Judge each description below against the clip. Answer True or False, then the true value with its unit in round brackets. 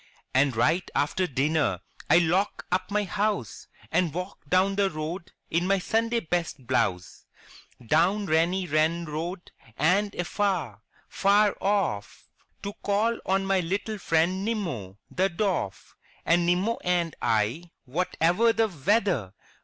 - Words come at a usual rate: False (130 wpm)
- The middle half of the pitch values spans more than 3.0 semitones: True (4.3 semitones)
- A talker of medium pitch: True (180 Hz)